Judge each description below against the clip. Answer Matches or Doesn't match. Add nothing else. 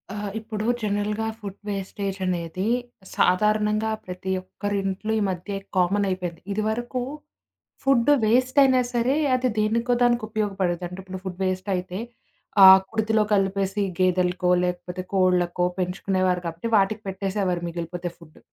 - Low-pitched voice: Doesn't match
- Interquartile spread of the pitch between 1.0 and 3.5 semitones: Matches